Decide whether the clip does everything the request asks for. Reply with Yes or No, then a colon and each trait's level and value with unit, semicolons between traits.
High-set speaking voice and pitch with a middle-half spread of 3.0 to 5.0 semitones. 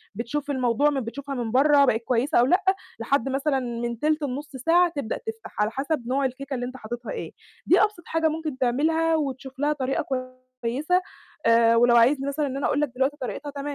Yes: very high, 275 Hz; average, 3.5 semitones